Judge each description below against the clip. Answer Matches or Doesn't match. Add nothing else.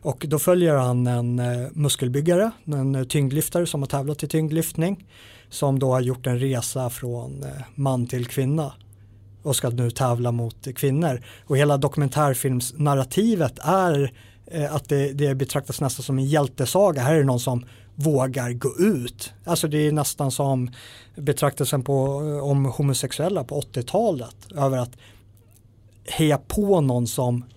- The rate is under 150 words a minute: Matches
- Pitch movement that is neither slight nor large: Matches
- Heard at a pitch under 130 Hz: Doesn't match